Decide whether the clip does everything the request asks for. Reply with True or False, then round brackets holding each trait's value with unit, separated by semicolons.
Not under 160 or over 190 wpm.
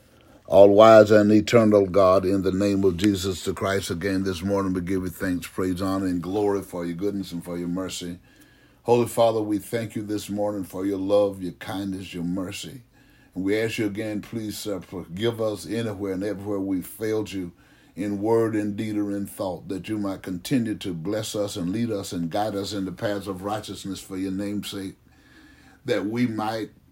False (200 wpm)